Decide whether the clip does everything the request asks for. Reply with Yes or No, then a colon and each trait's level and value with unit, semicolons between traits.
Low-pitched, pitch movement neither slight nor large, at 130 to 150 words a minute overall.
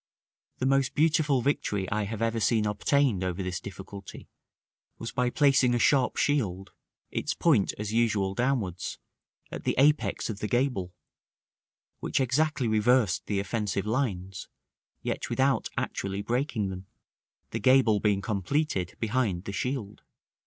Yes: low, 110 Hz; average, 5.0 semitones; average, 140 wpm